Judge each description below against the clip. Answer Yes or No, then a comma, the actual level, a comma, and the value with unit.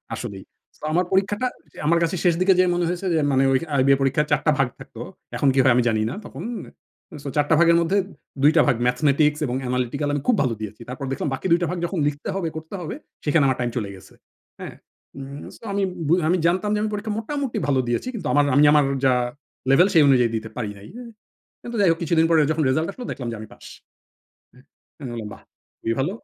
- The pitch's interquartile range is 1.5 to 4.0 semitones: No, average, 5.0 semitones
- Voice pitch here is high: No, medium, 150 Hz